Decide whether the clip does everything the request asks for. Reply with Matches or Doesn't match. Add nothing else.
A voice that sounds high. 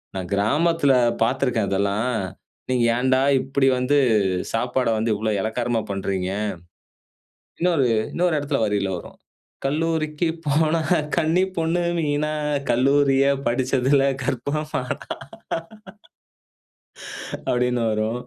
Doesn't match